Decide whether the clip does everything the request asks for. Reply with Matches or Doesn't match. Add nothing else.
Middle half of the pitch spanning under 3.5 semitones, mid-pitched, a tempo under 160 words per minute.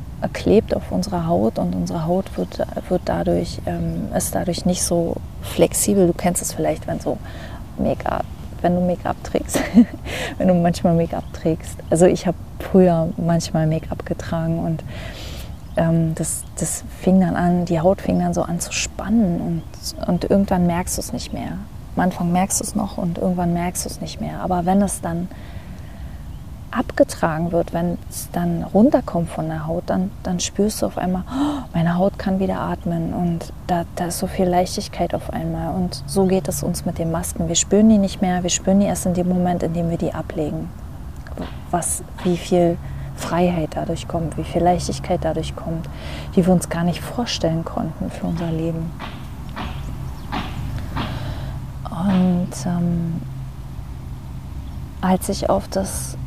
Doesn't match